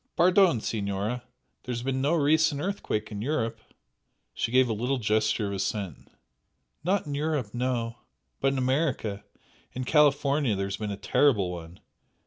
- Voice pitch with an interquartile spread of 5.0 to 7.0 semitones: Yes, average, 5.3 semitones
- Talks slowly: No, average, 155 wpm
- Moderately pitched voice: No, low, 125 Hz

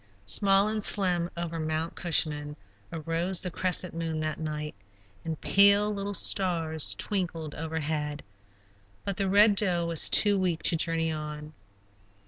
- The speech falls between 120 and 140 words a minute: Yes, slow, 135 wpm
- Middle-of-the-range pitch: Yes, medium, 165 Hz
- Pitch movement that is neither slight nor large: Yes, average, 3.5 semitones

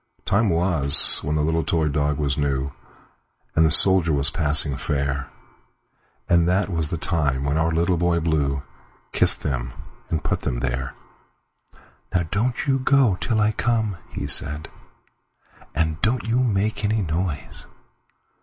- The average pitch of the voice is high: No, very low, 80 Hz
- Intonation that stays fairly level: No, average, 5.2 semitones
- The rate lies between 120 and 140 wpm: Yes, slow, 135 wpm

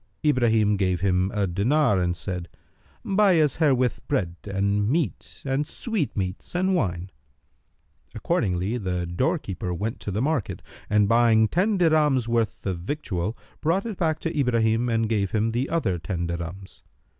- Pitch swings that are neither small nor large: No, wide, 7.7 semitones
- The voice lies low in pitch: Yes, low, 110 Hz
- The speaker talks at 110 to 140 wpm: No, average, 150 wpm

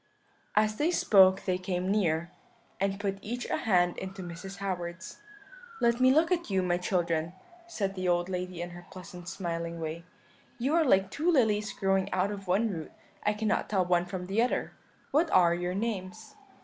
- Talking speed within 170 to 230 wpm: Yes, average, 185 wpm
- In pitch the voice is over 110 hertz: Yes, high, 190 Hz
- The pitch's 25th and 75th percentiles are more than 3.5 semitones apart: No, average, 3.2 semitones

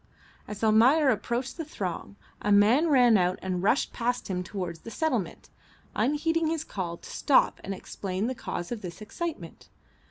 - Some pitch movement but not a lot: No, wide, 7.0 semitones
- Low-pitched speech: No, high, 220 Hz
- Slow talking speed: No, average, 165 wpm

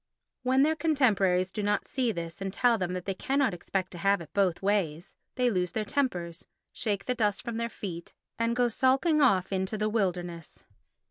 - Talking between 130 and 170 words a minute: No, average, 195 wpm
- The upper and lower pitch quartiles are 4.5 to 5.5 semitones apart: Yes, average, 5.2 semitones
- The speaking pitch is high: Yes, high, 205 Hz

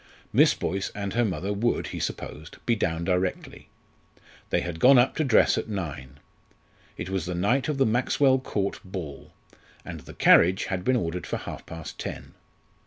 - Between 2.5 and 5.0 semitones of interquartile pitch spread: No, wide, 5.6 semitones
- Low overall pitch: Yes, very low, 95 Hz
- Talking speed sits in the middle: Yes, average, 175 wpm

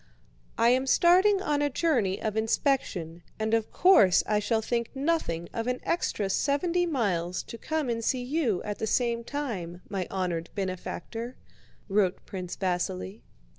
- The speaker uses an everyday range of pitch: No, wide, 6.8 semitones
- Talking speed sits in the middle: Yes, average, 155 wpm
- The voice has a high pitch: Yes, high, 225 Hz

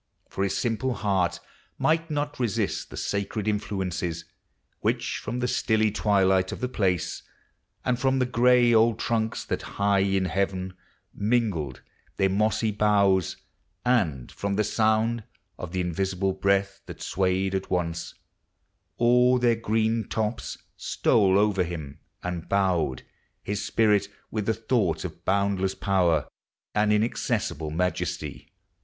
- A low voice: Yes, low, 100 Hz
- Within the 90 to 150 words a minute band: Yes, slow, 135 wpm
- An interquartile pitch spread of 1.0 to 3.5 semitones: Yes, average, 3.2 semitones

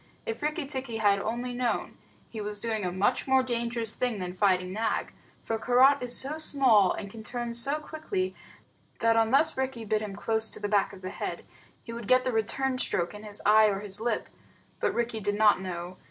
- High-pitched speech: Yes, high, 225 Hz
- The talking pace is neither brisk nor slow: No, fast, 210 wpm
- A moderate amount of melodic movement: Yes, average, 3.6 semitones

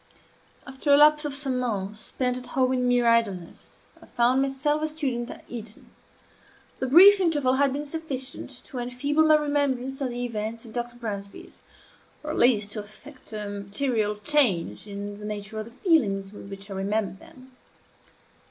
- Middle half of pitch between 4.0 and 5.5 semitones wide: Yes, average, 4.8 semitones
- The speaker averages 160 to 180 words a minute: Yes, average, 175 wpm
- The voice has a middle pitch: No, high, 245 Hz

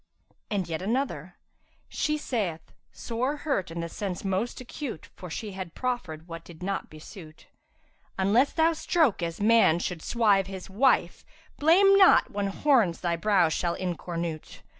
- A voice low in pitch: No, high, 195 Hz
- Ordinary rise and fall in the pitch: No, wide, 6.6 semitones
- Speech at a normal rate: Yes, average, 160 wpm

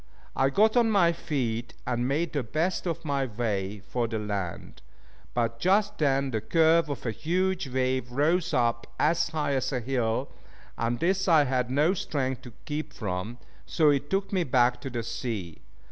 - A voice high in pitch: No, low, 135 Hz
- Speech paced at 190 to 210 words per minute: No, average, 180 wpm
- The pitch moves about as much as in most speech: No, wide, 5.7 semitones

